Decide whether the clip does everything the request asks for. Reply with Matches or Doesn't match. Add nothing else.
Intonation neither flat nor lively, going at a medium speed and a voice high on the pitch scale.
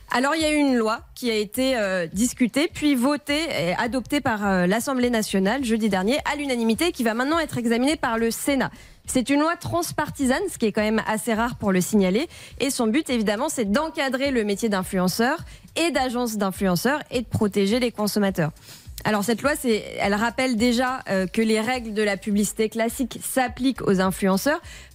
Matches